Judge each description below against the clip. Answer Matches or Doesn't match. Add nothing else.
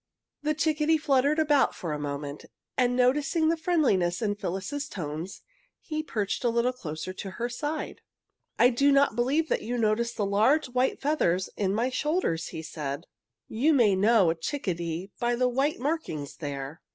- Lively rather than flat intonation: Matches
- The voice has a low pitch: Doesn't match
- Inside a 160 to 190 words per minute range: Matches